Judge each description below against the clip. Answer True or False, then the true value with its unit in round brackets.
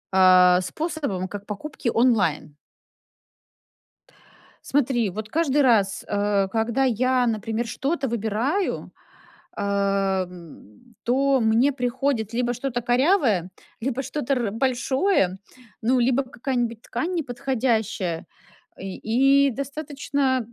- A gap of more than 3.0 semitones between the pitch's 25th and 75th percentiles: True (4.4 semitones)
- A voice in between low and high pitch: False (240 Hz)